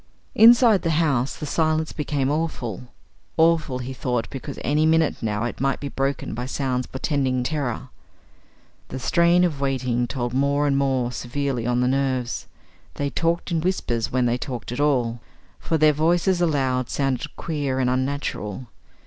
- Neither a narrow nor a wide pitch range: Yes, average, 3.7 semitones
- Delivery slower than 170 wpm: Yes, average, 160 wpm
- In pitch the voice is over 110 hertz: Yes, low, 135 Hz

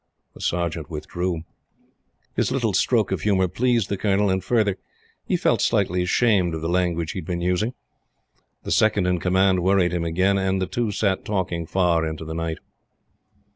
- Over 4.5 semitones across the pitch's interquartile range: No, narrow, 2.5 semitones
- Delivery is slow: No, average, 175 wpm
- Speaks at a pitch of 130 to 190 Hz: No, very low, 90 Hz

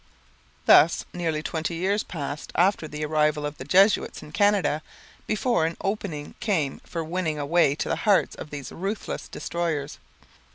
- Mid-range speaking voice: Yes, medium, 165 Hz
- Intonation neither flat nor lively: Yes, average, 4.1 semitones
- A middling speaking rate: Yes, average, 160 wpm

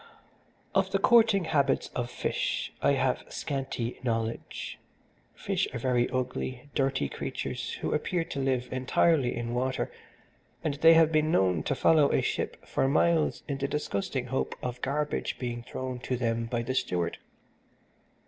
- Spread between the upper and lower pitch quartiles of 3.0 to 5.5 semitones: Yes, average, 3.7 semitones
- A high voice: No, low, 130 Hz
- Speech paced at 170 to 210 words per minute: No, average, 155 wpm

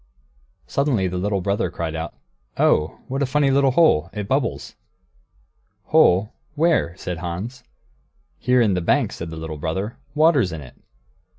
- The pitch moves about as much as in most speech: No, wide, 7.9 semitones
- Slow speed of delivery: No, average, 155 wpm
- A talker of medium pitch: No, low, 100 Hz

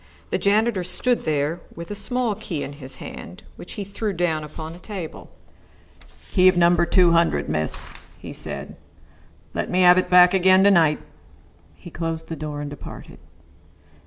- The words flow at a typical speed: Yes, average, 170 wpm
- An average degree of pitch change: Yes, average, 3.4 semitones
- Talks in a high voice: No, medium, 175 Hz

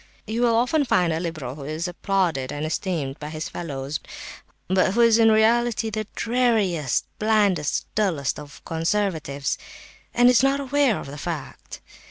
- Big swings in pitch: Yes, wide, 6.8 semitones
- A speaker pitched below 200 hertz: Yes, medium, 185 Hz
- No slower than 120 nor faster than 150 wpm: No, average, 160 wpm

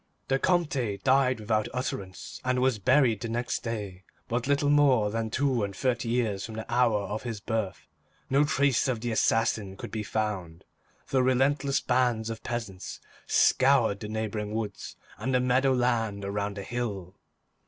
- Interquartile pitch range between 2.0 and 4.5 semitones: Yes, average, 3.6 semitones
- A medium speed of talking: Yes, average, 165 wpm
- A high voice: No, low, 115 Hz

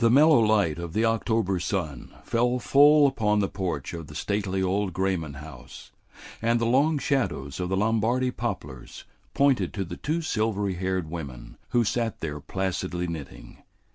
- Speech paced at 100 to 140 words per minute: No, average, 165 wpm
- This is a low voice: Yes, low, 100 Hz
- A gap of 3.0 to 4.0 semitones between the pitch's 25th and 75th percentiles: No, average, 5.3 semitones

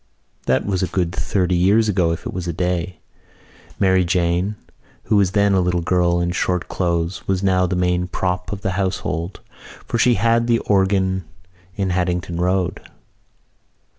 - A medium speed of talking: Yes, average, 165 wpm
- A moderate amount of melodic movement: No, narrow, 1.7 semitones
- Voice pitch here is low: Yes, very low, 90 Hz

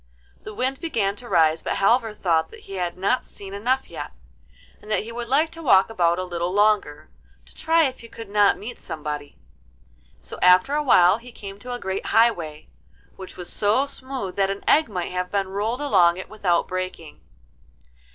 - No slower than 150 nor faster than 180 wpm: No, average, 195 wpm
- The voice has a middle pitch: No, high, 200 Hz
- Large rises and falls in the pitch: No, average, 4.8 semitones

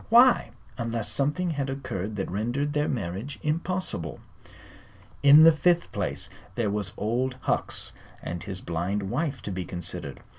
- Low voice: Yes, low, 120 Hz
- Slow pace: No, average, 145 wpm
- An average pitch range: No, wide, 7.0 semitones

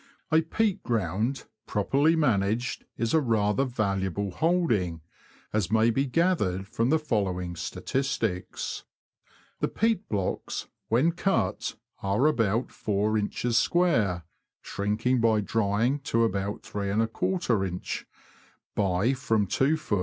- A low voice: Yes, low, 115 Hz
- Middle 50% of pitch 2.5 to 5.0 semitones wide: No, wide, 5.6 semitones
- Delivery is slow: Yes, slow, 110 wpm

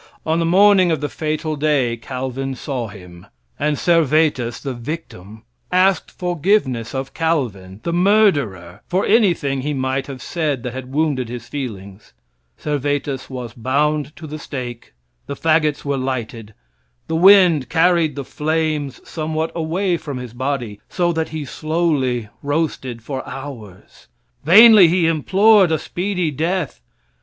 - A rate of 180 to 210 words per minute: No, average, 140 wpm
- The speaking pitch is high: No, medium, 145 Hz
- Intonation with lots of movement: No, average, 4.4 semitones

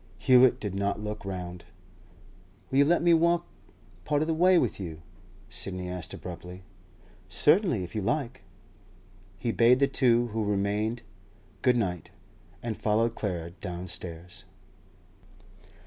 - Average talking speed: No, slow, 130 wpm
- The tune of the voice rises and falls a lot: Yes, wide, 6.0 semitones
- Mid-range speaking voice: No, low, 105 Hz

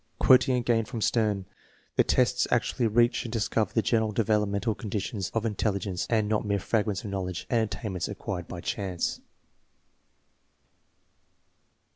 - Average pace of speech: Yes, average, 150 wpm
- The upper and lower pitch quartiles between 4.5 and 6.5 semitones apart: No, narrow, 2.6 semitones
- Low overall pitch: Yes, low, 110 Hz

